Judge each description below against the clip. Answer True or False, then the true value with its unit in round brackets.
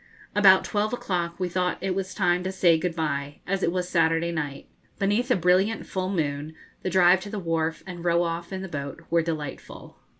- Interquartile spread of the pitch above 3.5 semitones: False (2.4 semitones)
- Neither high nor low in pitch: True (175 Hz)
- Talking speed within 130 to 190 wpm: False (205 wpm)